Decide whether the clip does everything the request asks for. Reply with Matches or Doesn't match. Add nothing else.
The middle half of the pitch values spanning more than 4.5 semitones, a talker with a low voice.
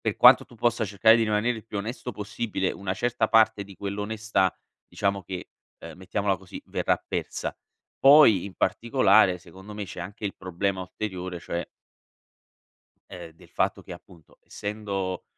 Doesn't match